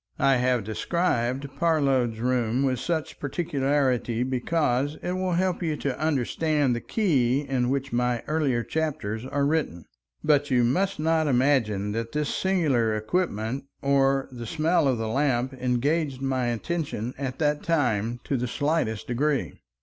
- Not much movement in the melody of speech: No, average, 4.0 semitones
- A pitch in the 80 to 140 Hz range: Yes, low, 135 Hz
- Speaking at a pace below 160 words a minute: Yes, average, 150 wpm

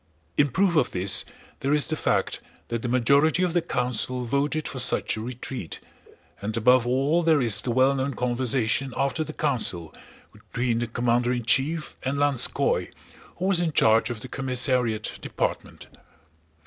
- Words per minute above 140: Yes, average, 165 wpm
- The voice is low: Yes, low, 130 Hz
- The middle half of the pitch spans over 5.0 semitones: No, average, 3.4 semitones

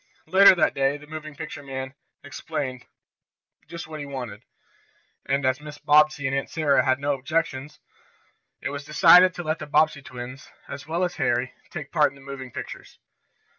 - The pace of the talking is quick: No, average, 175 wpm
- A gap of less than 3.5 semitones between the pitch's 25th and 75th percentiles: Yes, narrow, 2.5 semitones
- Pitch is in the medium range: Yes, medium, 145 Hz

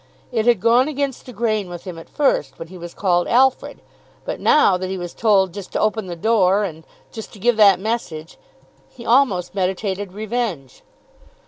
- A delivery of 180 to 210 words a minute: Yes, average, 190 wpm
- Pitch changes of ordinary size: Yes, average, 4.4 semitones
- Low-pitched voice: No, high, 205 Hz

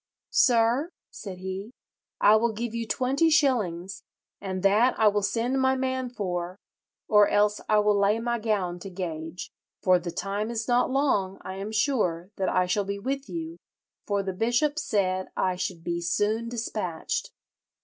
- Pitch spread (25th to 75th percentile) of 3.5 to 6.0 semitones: Yes, average, 4.2 semitones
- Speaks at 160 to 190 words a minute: Yes, average, 170 wpm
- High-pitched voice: Yes, high, 210 Hz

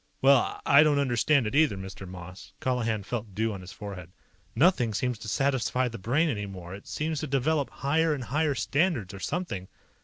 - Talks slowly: No, average, 185 wpm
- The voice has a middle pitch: No, low, 125 Hz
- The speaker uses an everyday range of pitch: No, wide, 6.0 semitones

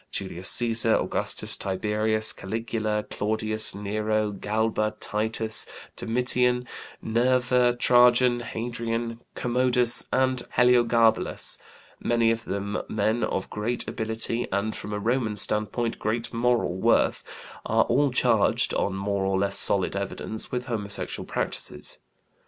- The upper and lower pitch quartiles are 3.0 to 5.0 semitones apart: No, narrow, 2.4 semitones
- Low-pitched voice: Yes, low, 115 Hz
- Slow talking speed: Yes, slow, 115 wpm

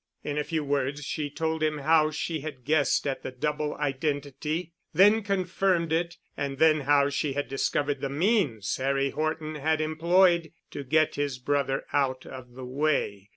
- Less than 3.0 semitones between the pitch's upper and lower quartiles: Yes, narrow, 2.5 semitones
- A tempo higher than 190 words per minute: No, average, 165 wpm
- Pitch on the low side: No, medium, 150 Hz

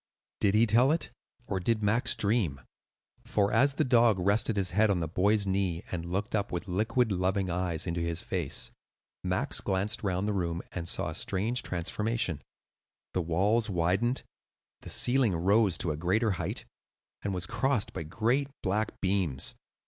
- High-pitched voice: No, low, 100 Hz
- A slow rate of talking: No, average, 165 wpm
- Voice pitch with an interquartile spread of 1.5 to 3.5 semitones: No, average, 3.9 semitones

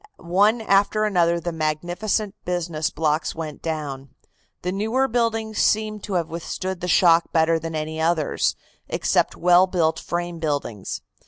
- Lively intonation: No, average, 3.8 semitones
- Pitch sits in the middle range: Yes, medium, 175 Hz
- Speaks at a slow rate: No, average, 150 wpm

